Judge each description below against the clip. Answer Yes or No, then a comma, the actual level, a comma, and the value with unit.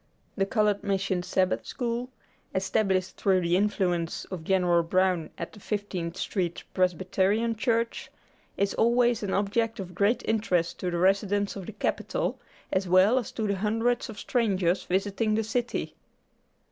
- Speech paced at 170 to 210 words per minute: No, average, 150 wpm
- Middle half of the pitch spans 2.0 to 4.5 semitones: Yes, average, 3.0 semitones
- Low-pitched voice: No, high, 200 Hz